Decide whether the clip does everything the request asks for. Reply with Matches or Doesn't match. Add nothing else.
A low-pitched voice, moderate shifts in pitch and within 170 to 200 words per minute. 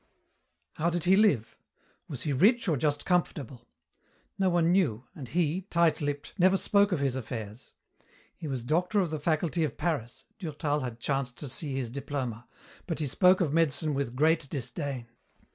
Doesn't match